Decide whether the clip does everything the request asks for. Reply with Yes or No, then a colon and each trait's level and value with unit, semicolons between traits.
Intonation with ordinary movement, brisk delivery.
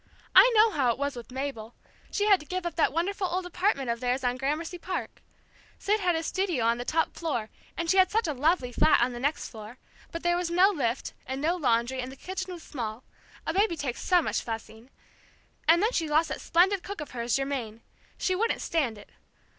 No: wide, 6.5 semitones; fast, 225 wpm